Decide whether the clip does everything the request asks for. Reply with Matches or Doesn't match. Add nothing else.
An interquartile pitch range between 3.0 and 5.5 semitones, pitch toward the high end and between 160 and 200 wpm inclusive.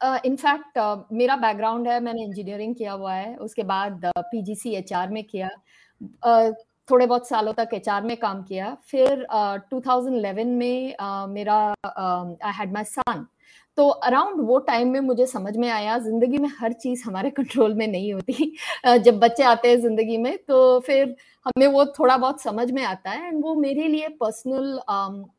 Matches